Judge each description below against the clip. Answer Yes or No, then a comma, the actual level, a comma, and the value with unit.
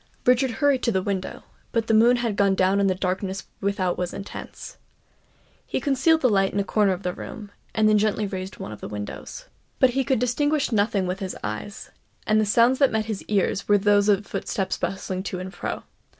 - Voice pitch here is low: No, high, 205 Hz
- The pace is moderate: No, fast, 215 wpm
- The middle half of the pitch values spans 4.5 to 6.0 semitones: No, average, 3.5 semitones